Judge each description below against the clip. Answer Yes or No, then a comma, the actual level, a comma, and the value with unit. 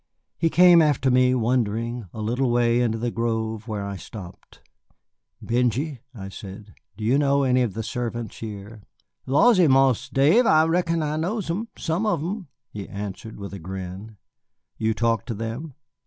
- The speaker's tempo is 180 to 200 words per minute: No, average, 170 wpm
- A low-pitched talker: Yes, low, 120 Hz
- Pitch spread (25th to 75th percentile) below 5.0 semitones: No, average, 5.3 semitones